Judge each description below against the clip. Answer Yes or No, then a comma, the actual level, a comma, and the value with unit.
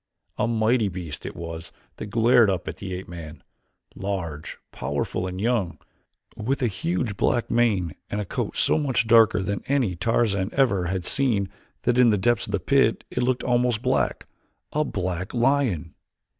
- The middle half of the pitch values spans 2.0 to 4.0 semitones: No, average, 4.8 semitones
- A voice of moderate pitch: No, low, 105 Hz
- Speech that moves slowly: No, average, 170 wpm